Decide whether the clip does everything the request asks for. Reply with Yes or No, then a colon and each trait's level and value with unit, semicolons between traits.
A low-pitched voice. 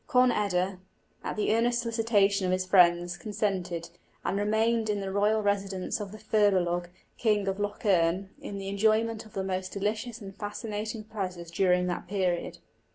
No: high, 200 Hz